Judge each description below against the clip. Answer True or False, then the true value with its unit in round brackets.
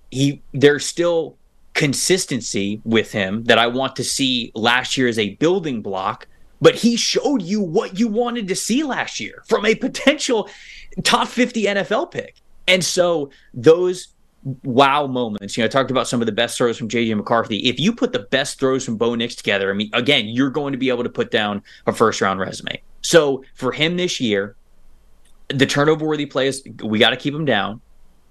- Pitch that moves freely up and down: True (7.7 semitones)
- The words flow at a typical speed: True (195 wpm)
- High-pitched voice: False (135 Hz)